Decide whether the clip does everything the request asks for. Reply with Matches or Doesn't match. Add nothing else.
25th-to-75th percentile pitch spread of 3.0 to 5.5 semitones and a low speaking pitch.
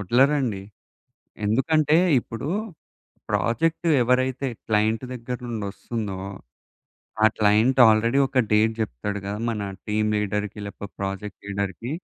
Matches